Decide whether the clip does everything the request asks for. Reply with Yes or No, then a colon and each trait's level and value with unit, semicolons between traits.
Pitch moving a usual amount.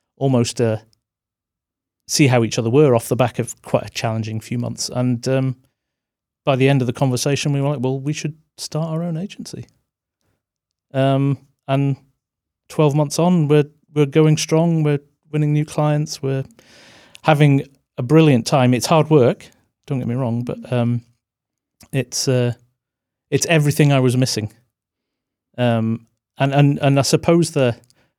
Yes: average, 3.7 semitones